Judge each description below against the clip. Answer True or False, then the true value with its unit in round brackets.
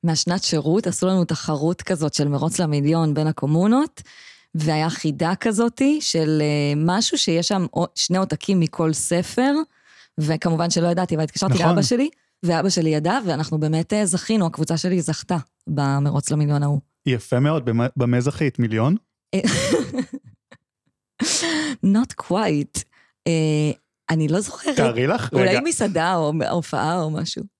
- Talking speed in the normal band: True (130 wpm)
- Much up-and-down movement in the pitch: False (3.6 semitones)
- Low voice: False (165 Hz)